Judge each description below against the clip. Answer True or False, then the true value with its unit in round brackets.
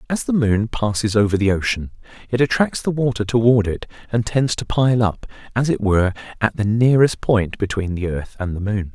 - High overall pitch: False (110 Hz)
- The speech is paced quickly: True (210 wpm)